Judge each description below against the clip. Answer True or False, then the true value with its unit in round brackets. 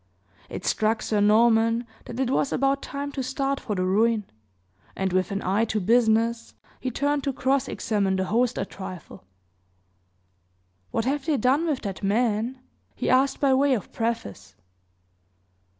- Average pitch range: True (4.4 semitones)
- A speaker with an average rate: True (160 wpm)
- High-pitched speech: True (230 Hz)